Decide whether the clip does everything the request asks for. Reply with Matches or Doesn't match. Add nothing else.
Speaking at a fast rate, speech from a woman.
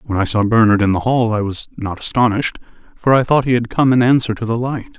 Doesn't match